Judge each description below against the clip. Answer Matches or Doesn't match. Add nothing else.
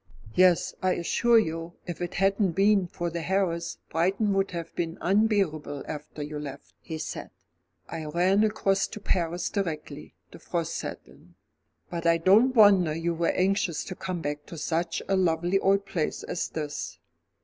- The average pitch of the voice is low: Doesn't match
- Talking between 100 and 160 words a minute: Doesn't match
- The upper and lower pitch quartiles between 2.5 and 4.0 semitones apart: Matches